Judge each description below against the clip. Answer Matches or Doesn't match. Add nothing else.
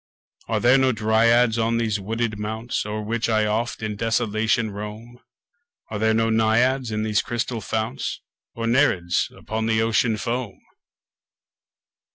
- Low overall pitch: Matches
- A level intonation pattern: Matches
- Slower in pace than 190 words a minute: Matches